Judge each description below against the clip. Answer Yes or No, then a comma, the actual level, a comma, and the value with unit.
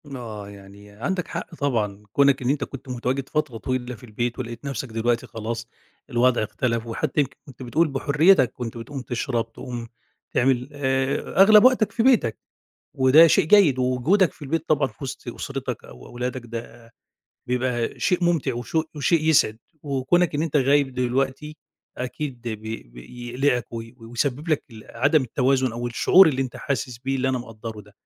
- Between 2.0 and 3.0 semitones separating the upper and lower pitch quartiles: No, average, 3.5 semitones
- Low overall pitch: Yes, low, 130 Hz